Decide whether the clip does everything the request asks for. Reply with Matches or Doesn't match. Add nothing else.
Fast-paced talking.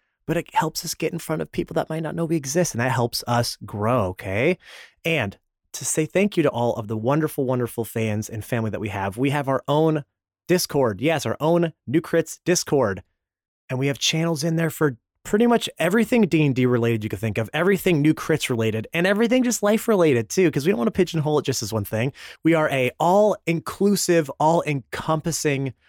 Matches